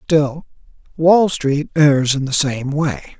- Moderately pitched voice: Yes, medium, 145 Hz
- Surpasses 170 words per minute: No, average, 150 wpm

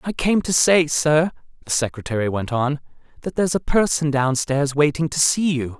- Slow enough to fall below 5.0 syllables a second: No, 5.1 syllables/s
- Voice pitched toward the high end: No, medium, 150 Hz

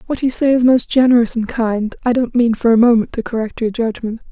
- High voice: Yes, high, 235 Hz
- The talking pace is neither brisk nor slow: No, fast, 250 wpm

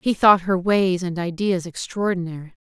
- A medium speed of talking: Yes, average, 160 wpm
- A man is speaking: No, female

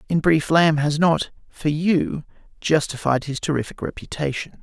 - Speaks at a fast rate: No, average, 145 wpm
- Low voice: No, medium, 155 Hz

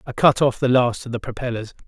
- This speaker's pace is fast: Yes, fast, 255 wpm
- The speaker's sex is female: No, male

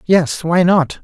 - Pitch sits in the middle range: Yes, medium, 170 Hz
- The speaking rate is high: No, average, 175 wpm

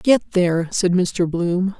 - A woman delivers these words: Yes, female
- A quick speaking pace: No, average, 165 wpm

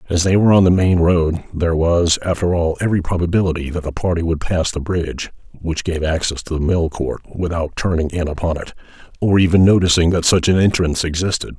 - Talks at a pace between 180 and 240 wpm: Yes, fast, 205 wpm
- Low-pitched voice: Yes, very low, 85 Hz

